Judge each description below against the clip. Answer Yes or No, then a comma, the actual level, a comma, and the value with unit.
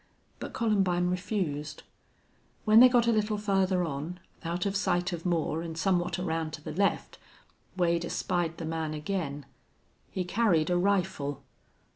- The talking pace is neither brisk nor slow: Yes, average, 150 wpm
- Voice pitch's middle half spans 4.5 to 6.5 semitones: No, average, 3.4 semitones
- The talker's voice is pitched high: No, medium, 175 Hz